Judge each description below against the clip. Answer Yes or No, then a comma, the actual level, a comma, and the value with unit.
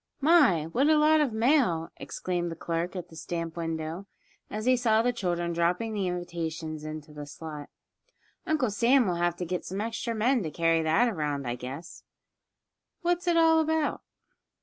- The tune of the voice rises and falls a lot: Yes, wide, 7.1 semitones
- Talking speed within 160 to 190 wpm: Yes, average, 175 wpm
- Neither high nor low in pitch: Yes, medium, 180 Hz